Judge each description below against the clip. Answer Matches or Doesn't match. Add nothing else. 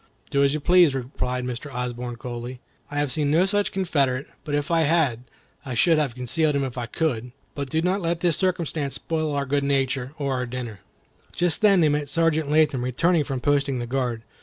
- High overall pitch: Doesn't match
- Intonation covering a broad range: Doesn't match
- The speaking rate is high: Matches